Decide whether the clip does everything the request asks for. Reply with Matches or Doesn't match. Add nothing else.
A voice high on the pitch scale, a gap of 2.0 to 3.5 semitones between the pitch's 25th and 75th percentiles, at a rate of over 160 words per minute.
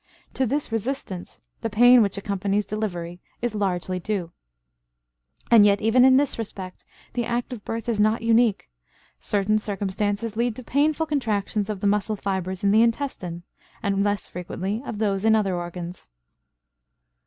Doesn't match